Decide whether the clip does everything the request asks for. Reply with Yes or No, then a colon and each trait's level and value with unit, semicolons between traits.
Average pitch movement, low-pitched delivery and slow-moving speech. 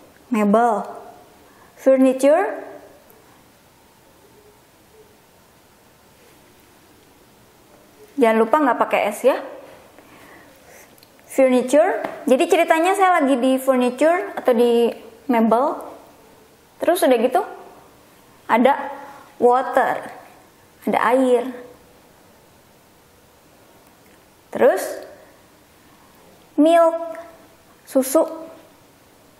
No: average, 4.8 semitones; very high, 275 Hz; slow, 55 wpm